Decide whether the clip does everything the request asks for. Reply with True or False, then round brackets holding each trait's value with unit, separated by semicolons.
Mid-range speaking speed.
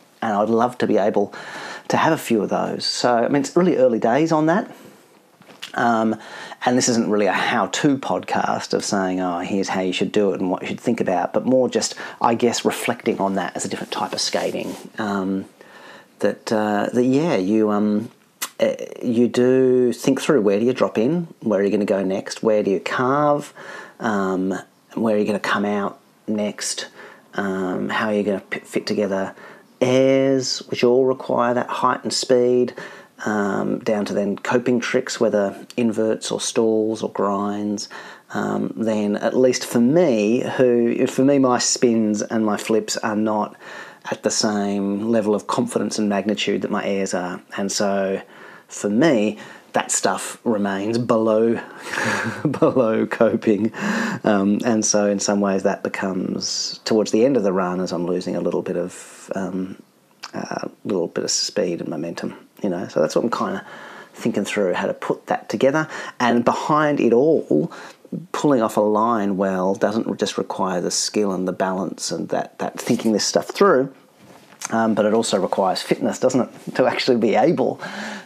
True (185 wpm)